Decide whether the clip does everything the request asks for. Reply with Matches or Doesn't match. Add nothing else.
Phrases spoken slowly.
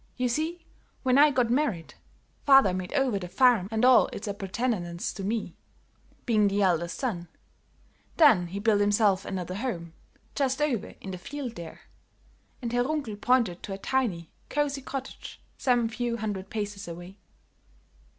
Doesn't match